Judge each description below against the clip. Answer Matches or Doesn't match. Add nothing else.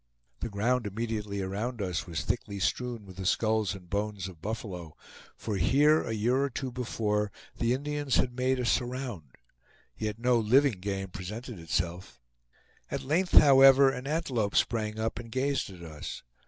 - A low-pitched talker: Matches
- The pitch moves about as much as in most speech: Matches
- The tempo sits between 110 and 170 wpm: Matches